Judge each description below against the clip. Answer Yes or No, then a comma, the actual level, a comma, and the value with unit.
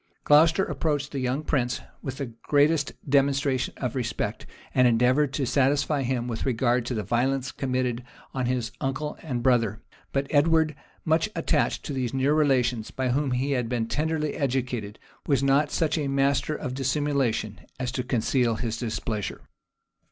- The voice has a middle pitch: No, low, 130 Hz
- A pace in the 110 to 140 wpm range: No, average, 160 wpm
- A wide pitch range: No, average, 2.8 semitones